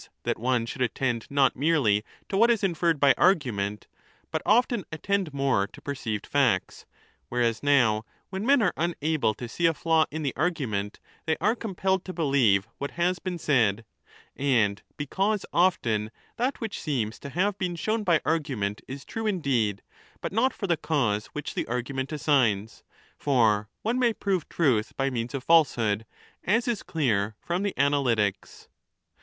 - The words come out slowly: No, average, 170 wpm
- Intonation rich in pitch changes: Yes, wide, 7.7 semitones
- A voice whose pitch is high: No, medium, 140 Hz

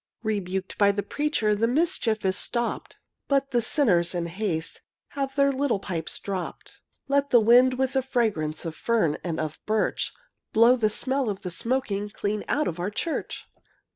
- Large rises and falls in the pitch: Yes, wide, 5.8 semitones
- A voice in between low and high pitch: No, high, 220 Hz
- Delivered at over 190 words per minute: No, average, 170 wpm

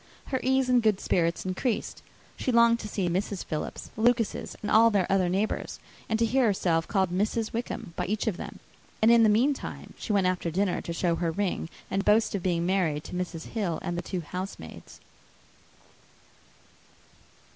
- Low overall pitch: No, high, 195 Hz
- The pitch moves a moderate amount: Yes, average, 4.1 semitones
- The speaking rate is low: No, average, 185 wpm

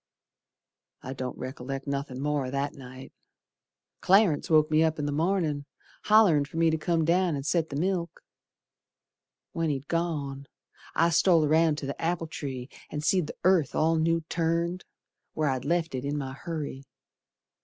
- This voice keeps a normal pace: Yes, average, 165 wpm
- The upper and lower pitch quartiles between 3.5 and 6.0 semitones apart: No, average, 3.1 semitones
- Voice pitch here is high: No, medium, 155 Hz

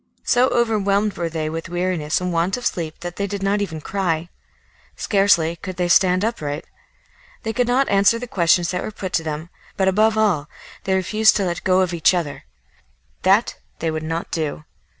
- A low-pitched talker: No, medium, 185 Hz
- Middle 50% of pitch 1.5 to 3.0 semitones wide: No, average, 3.5 semitones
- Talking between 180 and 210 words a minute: Yes, average, 190 wpm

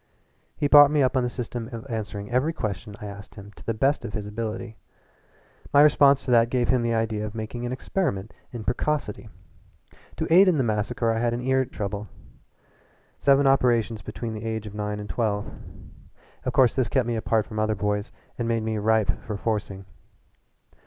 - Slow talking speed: No, average, 195 wpm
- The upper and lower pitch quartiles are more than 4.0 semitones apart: No, average, 3.1 semitones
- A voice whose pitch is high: No, low, 115 Hz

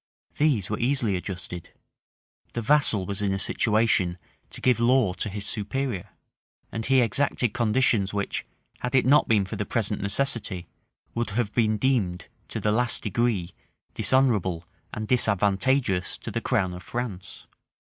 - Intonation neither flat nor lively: Yes, average, 4.2 semitones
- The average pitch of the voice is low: Yes, low, 110 Hz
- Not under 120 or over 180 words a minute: Yes, average, 150 wpm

